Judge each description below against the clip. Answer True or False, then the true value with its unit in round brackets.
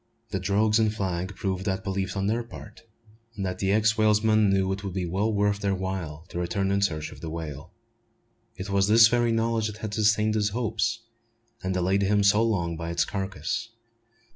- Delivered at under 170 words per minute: False (200 wpm)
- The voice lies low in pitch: True (100 Hz)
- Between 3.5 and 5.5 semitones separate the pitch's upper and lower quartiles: False (2.4 semitones)